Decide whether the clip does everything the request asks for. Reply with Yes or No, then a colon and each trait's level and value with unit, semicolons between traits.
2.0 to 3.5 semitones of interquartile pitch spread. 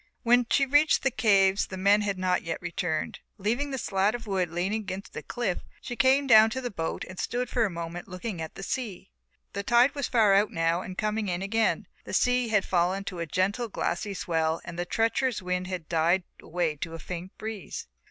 No: average, 4.4 semitones